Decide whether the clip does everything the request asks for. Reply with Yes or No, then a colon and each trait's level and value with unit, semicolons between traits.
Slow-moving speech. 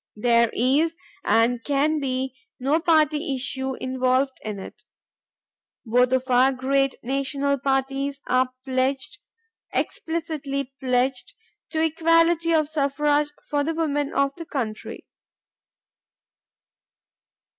Yes: slow, 105 wpm